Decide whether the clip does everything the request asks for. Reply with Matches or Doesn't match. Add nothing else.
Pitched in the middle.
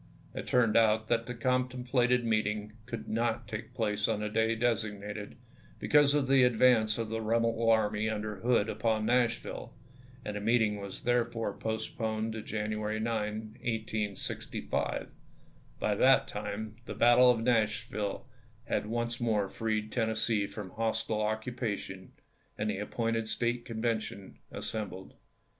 Doesn't match